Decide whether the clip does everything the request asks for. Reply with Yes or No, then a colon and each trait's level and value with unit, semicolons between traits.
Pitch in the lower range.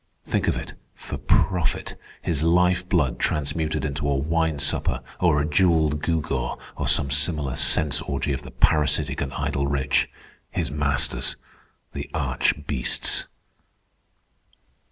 Yes: very low, 75 Hz